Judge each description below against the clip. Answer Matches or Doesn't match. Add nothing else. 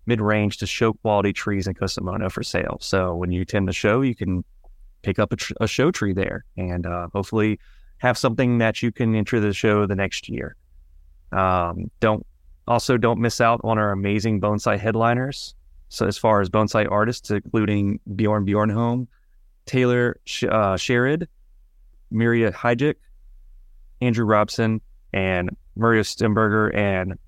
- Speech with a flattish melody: Doesn't match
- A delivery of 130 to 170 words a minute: Matches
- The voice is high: Doesn't match